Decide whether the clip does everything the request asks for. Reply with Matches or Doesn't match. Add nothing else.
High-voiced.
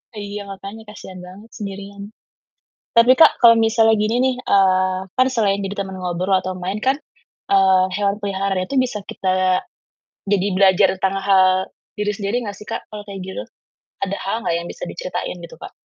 Matches